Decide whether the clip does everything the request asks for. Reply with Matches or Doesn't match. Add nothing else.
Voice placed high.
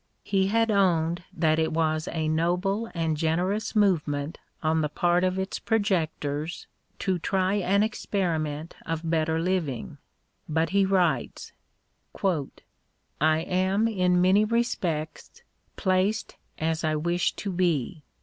Doesn't match